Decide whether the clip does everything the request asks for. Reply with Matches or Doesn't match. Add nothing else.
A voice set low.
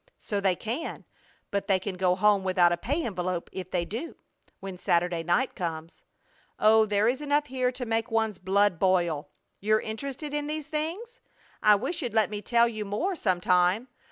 Doesn't match